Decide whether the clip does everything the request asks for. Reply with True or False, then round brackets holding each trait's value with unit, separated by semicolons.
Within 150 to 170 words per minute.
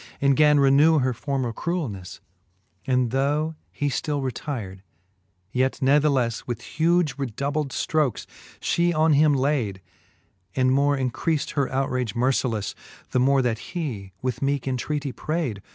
False (135 wpm)